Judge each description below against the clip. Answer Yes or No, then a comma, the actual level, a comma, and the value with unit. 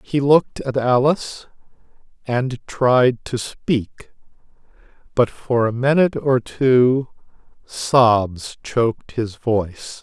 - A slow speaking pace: Yes, slow, 110 wpm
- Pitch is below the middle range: Yes, low, 120 Hz